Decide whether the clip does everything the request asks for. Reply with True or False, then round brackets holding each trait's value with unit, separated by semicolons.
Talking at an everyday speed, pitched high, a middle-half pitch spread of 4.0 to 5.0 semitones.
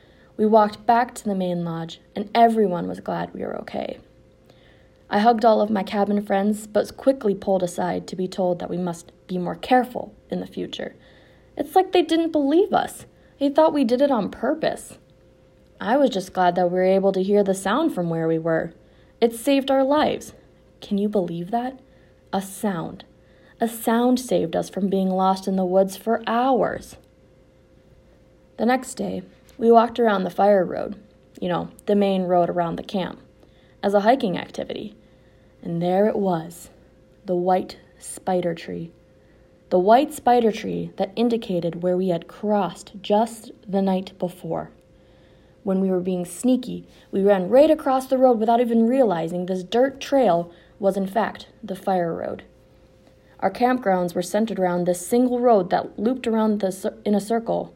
True (175 wpm; 205 Hz; 4.6 semitones)